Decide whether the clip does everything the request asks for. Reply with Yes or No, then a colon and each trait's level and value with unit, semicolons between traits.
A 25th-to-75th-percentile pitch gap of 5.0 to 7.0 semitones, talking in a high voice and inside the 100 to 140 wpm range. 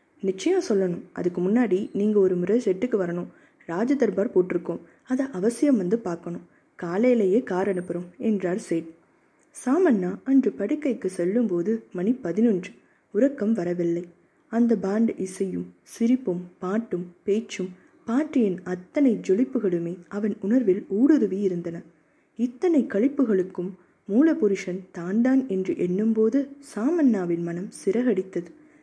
Yes: average, 5.3 semitones; high, 200 Hz; average, 105 wpm